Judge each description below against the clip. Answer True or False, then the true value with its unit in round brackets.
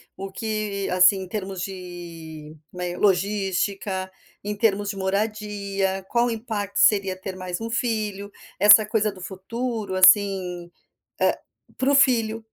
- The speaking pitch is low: False (200 Hz)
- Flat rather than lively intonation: True (2.3 semitones)